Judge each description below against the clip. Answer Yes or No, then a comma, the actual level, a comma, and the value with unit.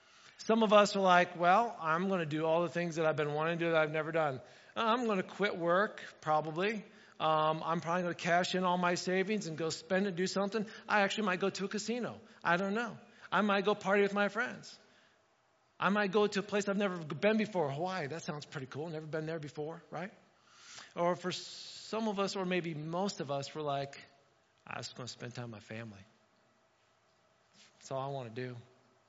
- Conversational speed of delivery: No, fast, 225 wpm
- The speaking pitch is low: No, medium, 175 Hz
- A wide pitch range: No, average, 4.3 semitones